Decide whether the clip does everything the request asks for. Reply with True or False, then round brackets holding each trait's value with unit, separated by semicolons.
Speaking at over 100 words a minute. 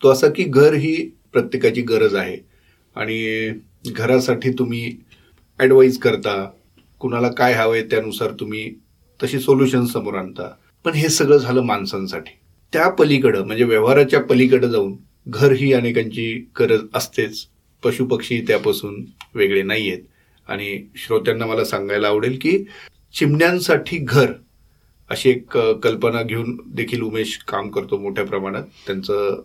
True (130 wpm)